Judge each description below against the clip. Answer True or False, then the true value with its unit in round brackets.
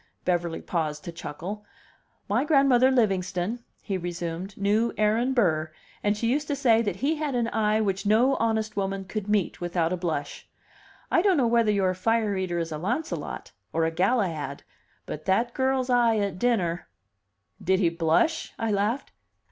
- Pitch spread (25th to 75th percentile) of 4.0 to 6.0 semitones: True (5.2 semitones)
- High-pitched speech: True (205 Hz)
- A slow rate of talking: False (170 wpm)